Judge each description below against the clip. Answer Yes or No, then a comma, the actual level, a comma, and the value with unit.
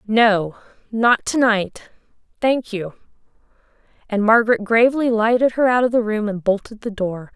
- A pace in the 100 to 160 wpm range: Yes, average, 155 wpm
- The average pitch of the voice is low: No, high, 220 Hz